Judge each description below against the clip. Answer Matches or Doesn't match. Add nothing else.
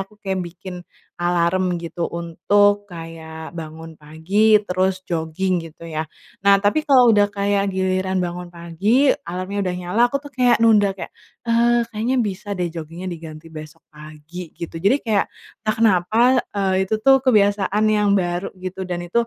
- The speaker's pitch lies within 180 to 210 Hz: Matches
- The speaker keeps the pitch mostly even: Doesn't match